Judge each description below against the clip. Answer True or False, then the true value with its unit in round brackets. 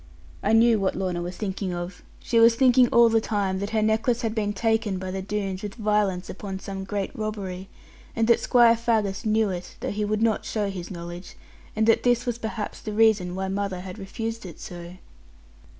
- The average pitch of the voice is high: True (210 Hz)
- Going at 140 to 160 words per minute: False (205 wpm)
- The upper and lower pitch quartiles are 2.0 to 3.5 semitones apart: True (2.9 semitones)